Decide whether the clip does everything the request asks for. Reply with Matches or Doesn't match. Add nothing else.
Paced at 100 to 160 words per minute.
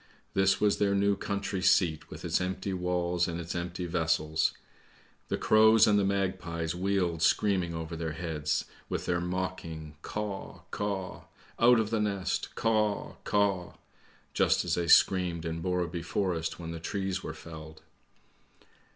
Matches